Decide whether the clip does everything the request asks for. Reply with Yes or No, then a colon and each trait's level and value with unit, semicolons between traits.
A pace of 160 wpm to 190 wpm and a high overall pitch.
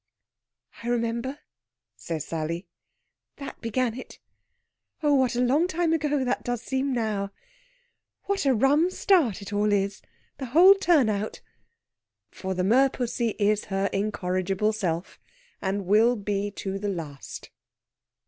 No: slow, 135 wpm; high, 220 Hz